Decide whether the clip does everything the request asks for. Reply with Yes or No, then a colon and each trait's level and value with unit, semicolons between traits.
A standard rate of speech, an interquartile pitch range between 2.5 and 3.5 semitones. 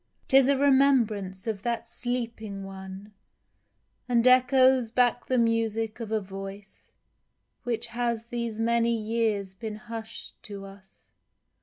No: slow, 125 wpm; average, 3.0 semitones